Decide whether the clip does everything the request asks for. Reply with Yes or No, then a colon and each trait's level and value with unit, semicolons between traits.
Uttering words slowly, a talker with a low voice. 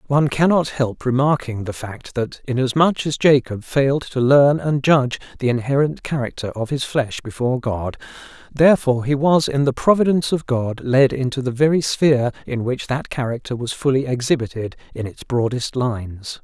No: average, 170 wpm; low, 130 Hz